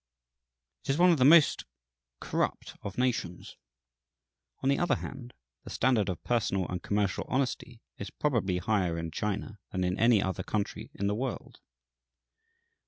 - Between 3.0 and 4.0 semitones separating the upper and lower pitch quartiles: No, average, 5.0 semitones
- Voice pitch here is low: Yes, low, 105 Hz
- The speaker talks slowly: No, average, 155 wpm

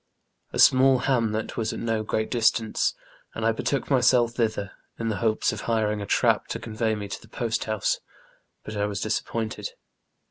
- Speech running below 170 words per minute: No, average, 175 wpm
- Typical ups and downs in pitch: No, narrow, 1.5 semitones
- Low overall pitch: Yes, low, 110 Hz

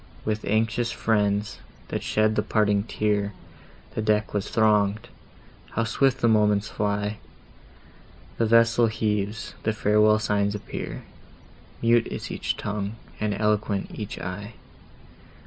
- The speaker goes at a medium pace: No, slow, 120 wpm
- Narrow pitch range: Yes, narrow, 1.3 semitones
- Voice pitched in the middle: No, low, 105 Hz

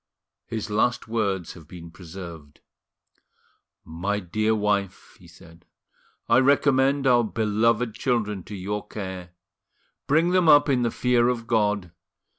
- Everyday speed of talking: No, slow, 130 wpm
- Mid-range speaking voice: No, low, 105 Hz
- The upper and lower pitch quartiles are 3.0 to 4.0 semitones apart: No, average, 4.7 semitones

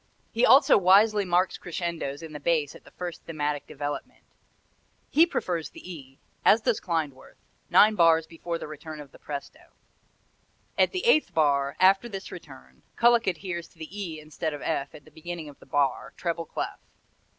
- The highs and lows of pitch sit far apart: No, average, 4.1 semitones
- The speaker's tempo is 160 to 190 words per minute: Yes, average, 175 wpm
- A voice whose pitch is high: No, medium, 165 Hz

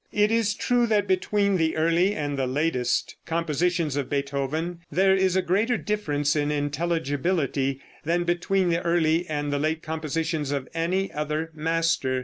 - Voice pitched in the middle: Yes, medium, 165 Hz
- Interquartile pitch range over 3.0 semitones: Yes, average, 3.9 semitones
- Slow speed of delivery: No, average, 155 wpm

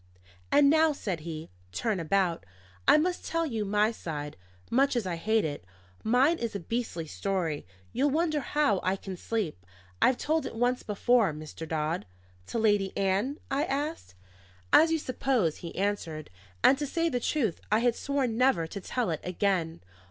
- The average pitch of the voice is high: Yes, high, 215 Hz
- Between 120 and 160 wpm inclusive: No, average, 175 wpm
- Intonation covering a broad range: Yes, wide, 7.8 semitones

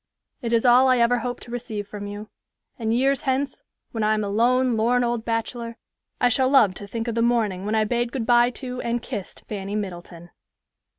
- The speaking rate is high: Yes, fast, 215 wpm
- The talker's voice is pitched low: No, high, 235 Hz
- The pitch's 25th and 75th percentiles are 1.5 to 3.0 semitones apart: Yes, narrow, 2.5 semitones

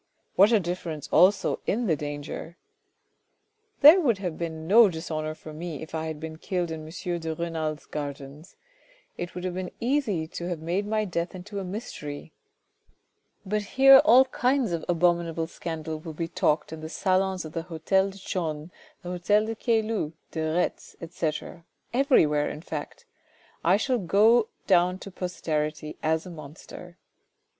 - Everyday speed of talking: Yes, average, 165 wpm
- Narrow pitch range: No, average, 3.9 semitones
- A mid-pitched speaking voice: Yes, medium, 175 Hz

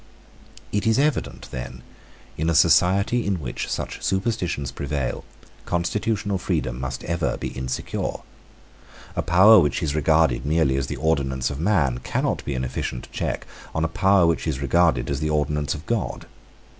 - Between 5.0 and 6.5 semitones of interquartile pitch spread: Yes, wide, 5.6 semitones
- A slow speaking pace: No, average, 160 wpm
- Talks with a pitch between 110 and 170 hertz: No, very low, 80 Hz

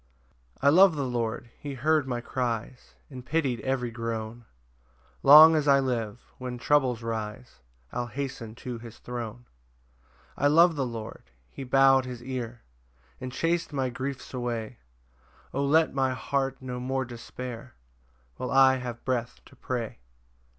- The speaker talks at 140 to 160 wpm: Yes, average, 150 wpm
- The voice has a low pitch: Yes, low, 125 Hz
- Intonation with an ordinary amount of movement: No, narrow, 2.3 semitones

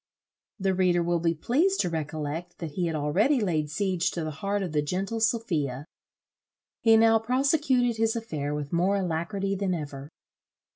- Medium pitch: Yes, medium, 180 Hz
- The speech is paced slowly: No, average, 165 wpm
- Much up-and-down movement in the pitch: Yes, wide, 6.0 semitones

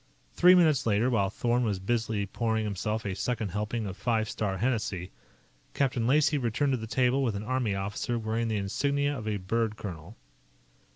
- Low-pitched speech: Yes, low, 110 Hz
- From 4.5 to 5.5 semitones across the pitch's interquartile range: No, average, 3.4 semitones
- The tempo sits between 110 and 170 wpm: No, average, 180 wpm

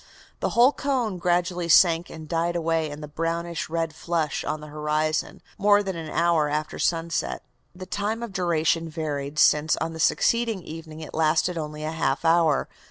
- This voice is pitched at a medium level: Yes, medium, 165 Hz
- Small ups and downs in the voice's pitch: Yes, narrow, 2.2 semitones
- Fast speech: No, average, 175 wpm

